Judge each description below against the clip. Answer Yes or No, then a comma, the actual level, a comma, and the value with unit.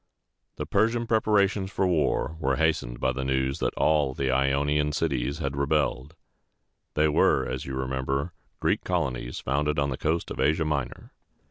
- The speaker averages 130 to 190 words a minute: Yes, average, 155 wpm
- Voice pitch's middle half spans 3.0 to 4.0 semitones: Yes, average, 3.3 semitones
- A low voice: Yes, very low, 70 Hz